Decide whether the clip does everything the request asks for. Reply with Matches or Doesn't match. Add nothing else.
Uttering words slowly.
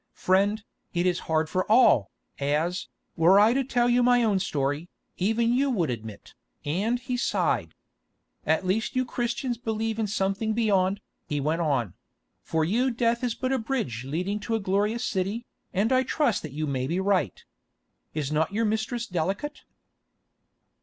Doesn't match